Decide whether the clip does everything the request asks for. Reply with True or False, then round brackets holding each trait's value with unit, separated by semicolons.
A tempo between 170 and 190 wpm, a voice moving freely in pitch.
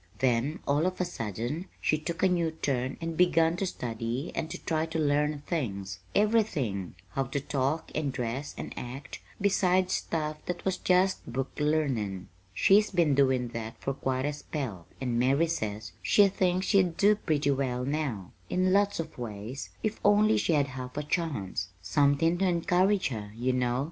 True (175 wpm; 6.0 semitones)